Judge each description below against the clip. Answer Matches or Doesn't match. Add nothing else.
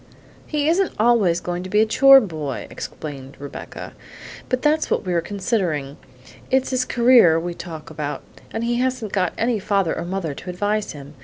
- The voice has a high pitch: Matches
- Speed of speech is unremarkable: Matches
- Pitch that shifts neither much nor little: Doesn't match